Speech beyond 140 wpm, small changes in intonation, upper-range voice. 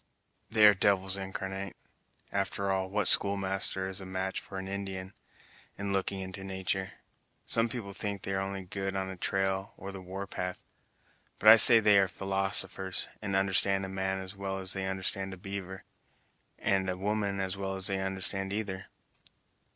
No: average, 180 wpm; narrow, 0.6 semitones; very low, 95 Hz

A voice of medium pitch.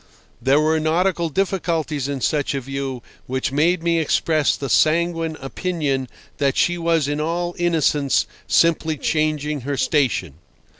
Yes: medium, 155 Hz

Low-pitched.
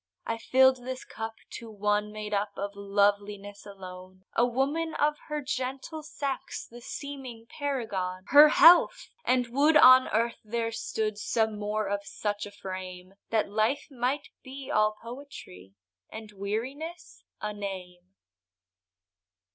No: high, 220 Hz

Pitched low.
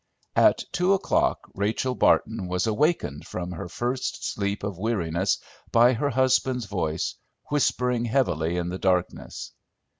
Yes: low, 105 Hz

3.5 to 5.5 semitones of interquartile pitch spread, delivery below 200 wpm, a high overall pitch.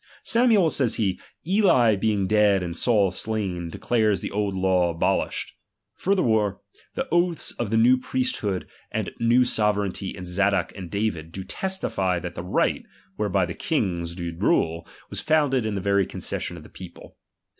No: average, 4.8 semitones; average, 160 wpm; low, 105 Hz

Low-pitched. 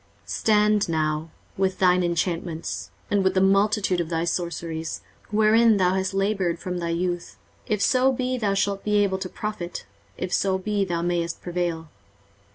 No: medium, 185 Hz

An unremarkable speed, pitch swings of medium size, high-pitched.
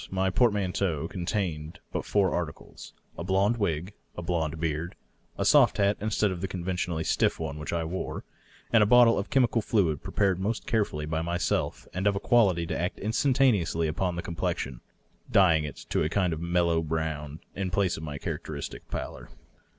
No: average, 185 wpm; average, 3.8 semitones; very low, 90 Hz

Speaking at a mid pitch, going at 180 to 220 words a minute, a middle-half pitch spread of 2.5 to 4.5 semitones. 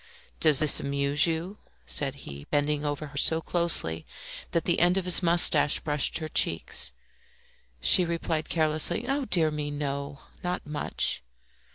No: medium, 155 Hz; average, 150 wpm; average, 2.9 semitones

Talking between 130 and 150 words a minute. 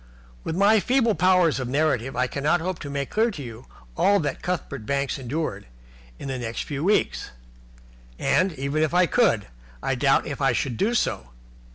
No: average, 185 wpm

